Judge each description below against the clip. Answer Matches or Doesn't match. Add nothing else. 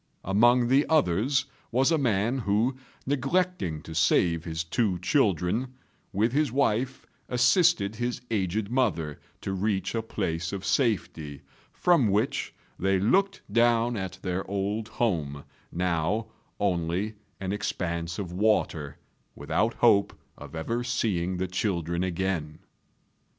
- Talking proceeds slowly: Matches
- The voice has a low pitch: Matches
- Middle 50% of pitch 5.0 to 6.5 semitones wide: Matches